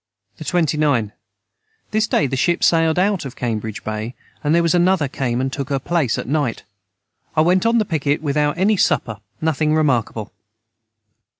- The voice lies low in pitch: No, medium, 150 Hz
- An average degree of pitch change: Yes, average, 4.9 semitones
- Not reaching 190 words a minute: Yes, average, 170 wpm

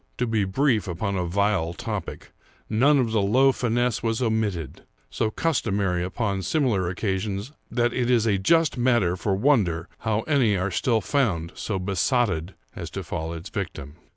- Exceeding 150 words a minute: Yes, average, 165 wpm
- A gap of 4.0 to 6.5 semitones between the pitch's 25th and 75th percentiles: Yes, average, 4.6 semitones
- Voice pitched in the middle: No, low, 105 Hz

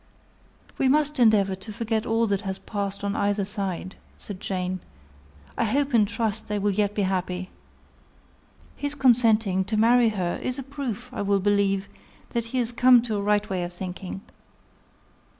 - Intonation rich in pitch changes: No, average, 3.2 semitones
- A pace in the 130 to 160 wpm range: No, average, 170 wpm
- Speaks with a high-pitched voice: Yes, high, 210 Hz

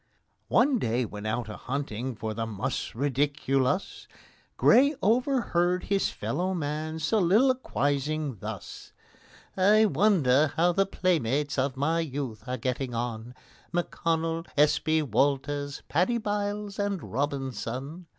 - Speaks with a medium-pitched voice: Yes, medium, 150 Hz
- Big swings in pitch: Yes, wide, 6.1 semitones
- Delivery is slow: Yes, slow, 120 wpm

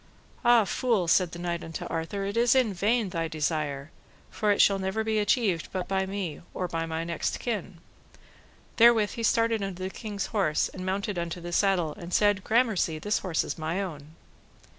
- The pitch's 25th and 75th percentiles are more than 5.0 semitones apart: No, average, 4.0 semitones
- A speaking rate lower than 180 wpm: No, average, 185 wpm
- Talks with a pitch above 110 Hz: Yes, high, 190 Hz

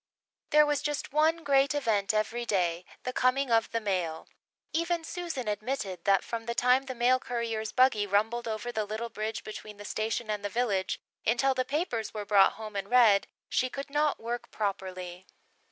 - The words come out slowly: No, average, 185 wpm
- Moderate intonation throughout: Yes, average, 4.0 semitones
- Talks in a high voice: Yes, high, 230 Hz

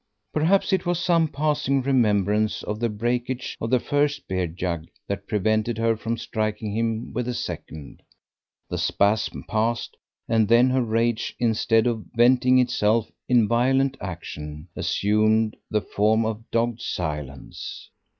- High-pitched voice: No, low, 115 Hz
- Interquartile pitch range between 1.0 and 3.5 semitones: Yes, average, 2.9 semitones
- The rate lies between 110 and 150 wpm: Yes, average, 140 wpm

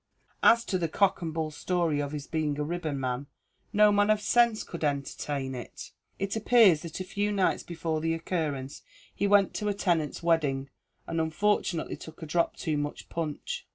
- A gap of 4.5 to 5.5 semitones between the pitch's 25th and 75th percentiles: Yes, average, 5.2 semitones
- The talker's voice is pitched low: No, medium, 165 Hz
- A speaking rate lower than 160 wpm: No, average, 185 wpm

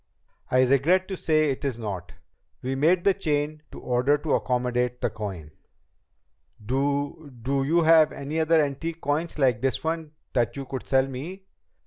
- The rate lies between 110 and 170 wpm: Yes, average, 165 wpm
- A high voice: No, medium, 140 Hz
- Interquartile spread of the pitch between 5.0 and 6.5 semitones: No, average, 3.8 semitones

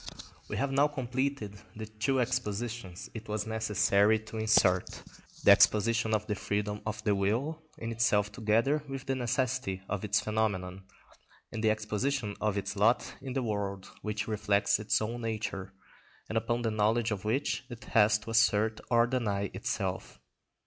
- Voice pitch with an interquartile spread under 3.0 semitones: Yes, narrow, 2.5 semitones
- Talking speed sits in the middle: Yes, average, 165 wpm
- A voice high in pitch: No, low, 110 Hz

